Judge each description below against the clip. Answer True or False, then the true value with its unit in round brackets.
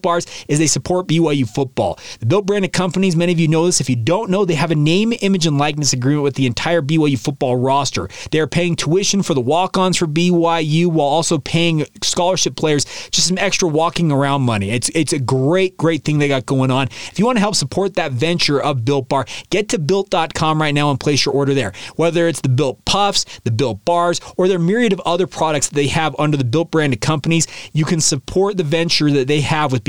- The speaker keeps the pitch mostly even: False (3.7 semitones)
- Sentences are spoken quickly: True (235 wpm)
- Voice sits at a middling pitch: True (160 Hz)